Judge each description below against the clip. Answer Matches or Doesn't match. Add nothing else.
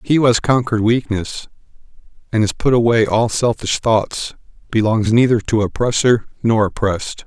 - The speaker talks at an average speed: Matches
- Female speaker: Doesn't match